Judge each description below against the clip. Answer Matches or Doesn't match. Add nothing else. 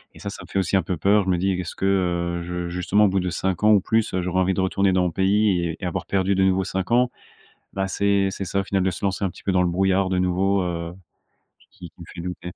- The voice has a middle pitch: Doesn't match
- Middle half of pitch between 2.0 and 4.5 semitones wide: Doesn't match